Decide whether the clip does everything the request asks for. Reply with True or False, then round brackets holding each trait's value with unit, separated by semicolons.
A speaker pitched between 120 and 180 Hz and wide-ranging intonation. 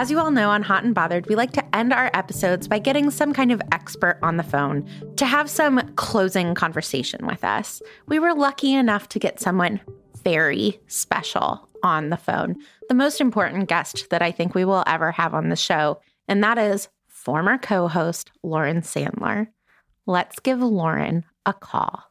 False (200 Hz; 6.8 semitones)